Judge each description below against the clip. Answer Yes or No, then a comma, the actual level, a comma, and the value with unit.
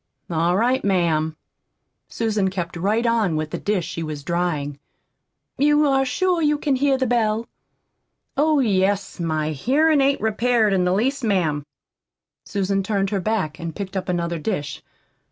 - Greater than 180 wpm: No, average, 155 wpm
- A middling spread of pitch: No, wide, 6.5 semitones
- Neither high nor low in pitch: No, high, 200 Hz